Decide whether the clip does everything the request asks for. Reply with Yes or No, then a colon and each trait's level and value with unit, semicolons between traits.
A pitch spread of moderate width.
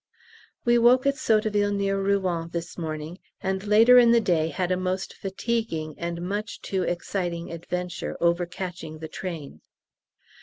Yes: average, 3.5 semitones